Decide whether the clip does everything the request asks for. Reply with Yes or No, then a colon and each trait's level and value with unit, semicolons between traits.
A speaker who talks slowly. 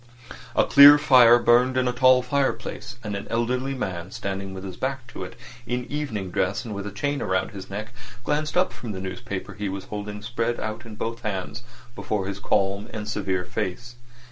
No: average, 195 wpm